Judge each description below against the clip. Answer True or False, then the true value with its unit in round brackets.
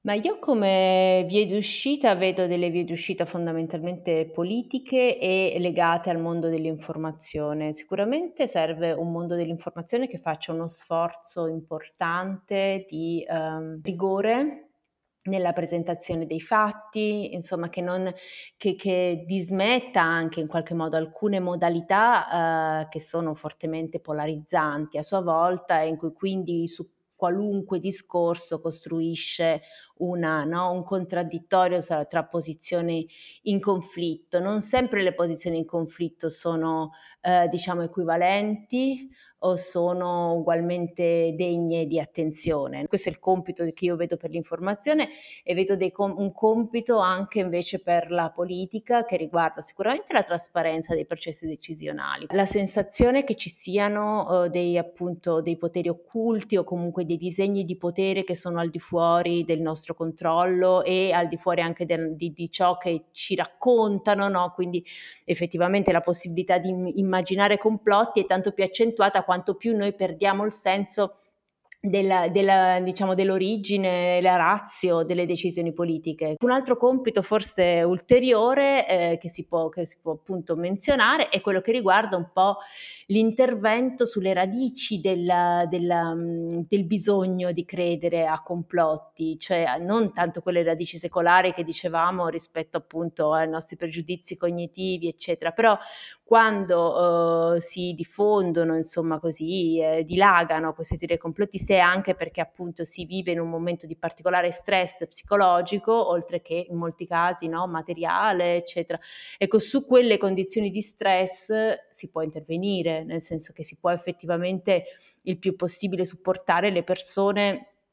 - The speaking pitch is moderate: True (175 Hz)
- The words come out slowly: False (140 wpm)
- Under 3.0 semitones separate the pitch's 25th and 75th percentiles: True (2.6 semitones)